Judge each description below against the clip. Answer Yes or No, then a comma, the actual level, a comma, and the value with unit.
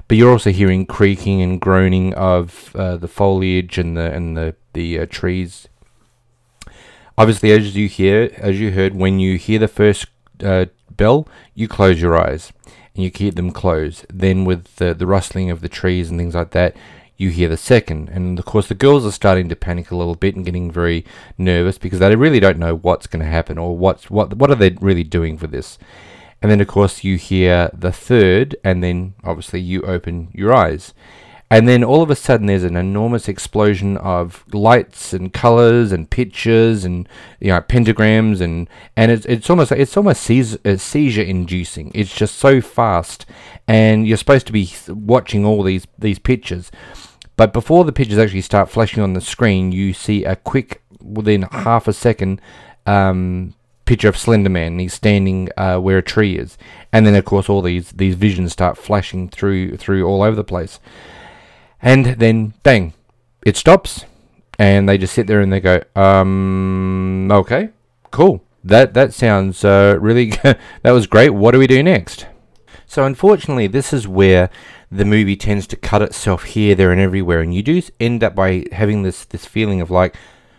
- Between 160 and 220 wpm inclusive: Yes, average, 190 wpm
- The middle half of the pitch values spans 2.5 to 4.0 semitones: Yes, average, 3.4 semitones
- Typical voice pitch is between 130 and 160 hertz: No, low, 100 Hz